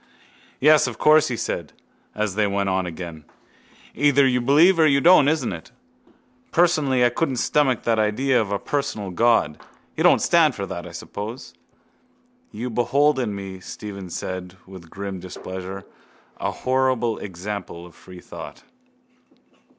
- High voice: No, low, 110 Hz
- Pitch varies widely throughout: Yes, wide, 6.4 semitones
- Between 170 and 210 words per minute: No, average, 150 wpm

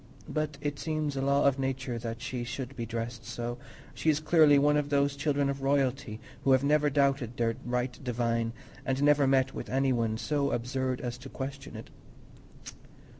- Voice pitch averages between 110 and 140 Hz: Yes, low, 135 Hz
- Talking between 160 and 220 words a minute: Yes, average, 185 wpm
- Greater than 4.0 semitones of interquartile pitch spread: No, narrow, 2.6 semitones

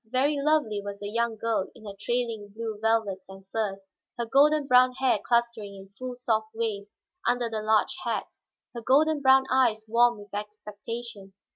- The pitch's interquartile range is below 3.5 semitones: Yes, average, 3.1 semitones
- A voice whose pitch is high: Yes, high, 225 Hz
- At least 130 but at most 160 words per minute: No, average, 170 wpm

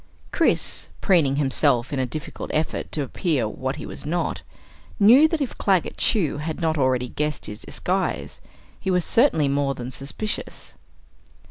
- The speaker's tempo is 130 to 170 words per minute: Yes, average, 155 wpm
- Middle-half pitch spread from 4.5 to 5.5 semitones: Yes, average, 5.1 semitones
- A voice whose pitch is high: No, medium, 150 Hz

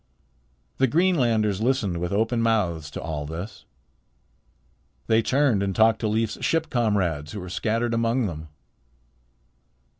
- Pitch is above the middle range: No, low, 110 Hz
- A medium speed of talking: No, slow, 130 wpm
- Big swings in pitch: No, average, 4.4 semitones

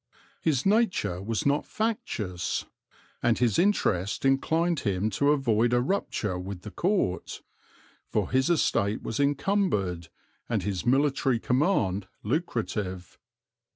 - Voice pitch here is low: Yes, low, 120 Hz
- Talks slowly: Yes, slow, 120 wpm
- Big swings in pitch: Yes, wide, 7.2 semitones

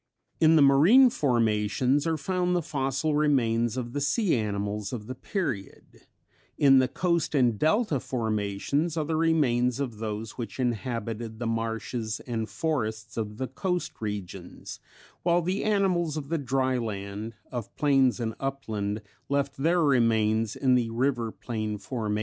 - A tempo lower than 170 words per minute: Yes, average, 150 wpm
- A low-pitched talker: Yes, low, 125 Hz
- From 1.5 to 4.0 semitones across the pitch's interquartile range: No, average, 5.1 semitones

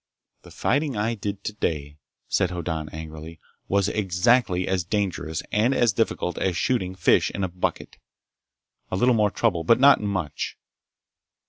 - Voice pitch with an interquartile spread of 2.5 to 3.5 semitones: No, average, 4.1 semitones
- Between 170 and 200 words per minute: No, average, 145 wpm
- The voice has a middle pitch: No, very low, 95 Hz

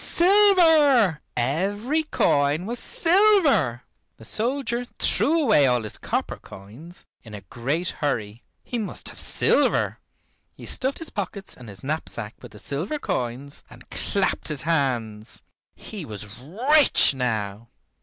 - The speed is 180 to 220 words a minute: No, slow, 135 wpm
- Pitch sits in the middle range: Yes, medium, 155 Hz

